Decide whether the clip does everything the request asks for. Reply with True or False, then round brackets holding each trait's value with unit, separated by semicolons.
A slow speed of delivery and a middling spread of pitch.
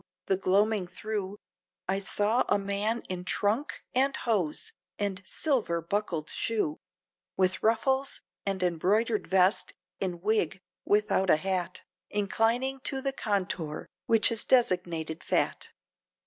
True (120 wpm; 3.5 semitones)